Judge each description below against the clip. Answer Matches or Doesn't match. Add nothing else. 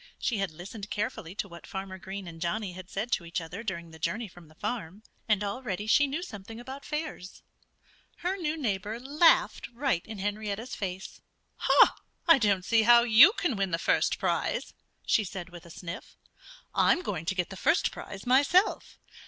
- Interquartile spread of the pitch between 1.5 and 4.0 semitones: Doesn't match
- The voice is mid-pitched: Doesn't match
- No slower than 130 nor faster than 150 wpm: Doesn't match